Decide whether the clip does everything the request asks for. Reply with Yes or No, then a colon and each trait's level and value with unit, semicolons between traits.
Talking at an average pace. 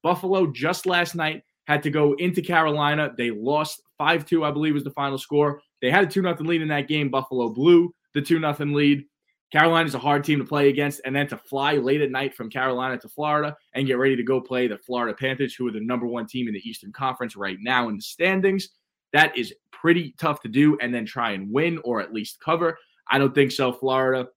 No: fast, 240 wpm